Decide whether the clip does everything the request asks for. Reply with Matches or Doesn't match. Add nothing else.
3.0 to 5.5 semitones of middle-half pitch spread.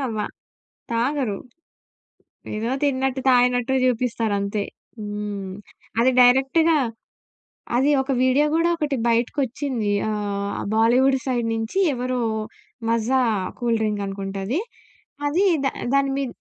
Matches